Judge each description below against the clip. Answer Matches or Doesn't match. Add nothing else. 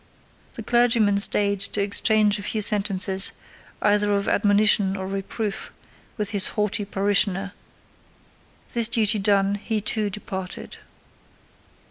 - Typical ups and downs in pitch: Doesn't match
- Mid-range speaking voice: Doesn't match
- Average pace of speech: Doesn't match